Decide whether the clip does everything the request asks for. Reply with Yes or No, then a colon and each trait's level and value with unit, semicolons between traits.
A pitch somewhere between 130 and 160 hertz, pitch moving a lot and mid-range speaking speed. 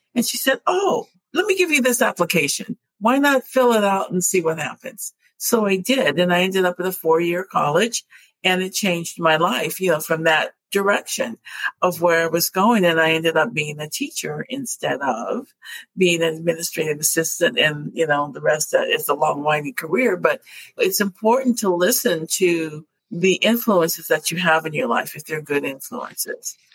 No: medium, 180 Hz; wide, 6.3 semitones; average, 195 wpm